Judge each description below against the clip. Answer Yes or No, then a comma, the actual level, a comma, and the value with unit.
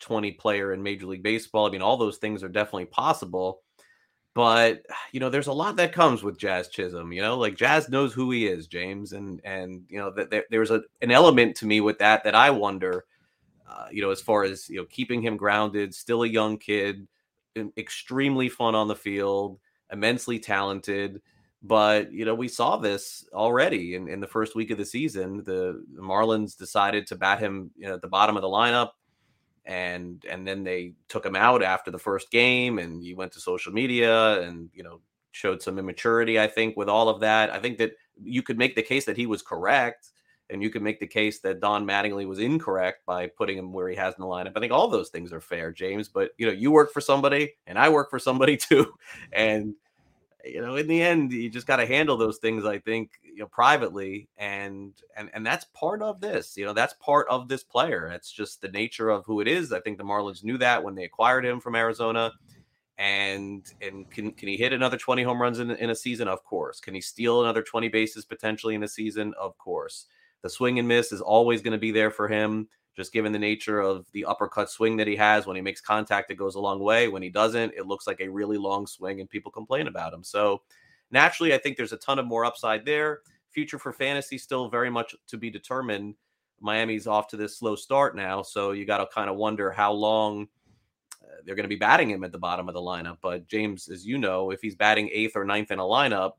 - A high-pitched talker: No, low, 105 Hz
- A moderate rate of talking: No, fast, 235 wpm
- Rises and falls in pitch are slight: No, average, 3.0 semitones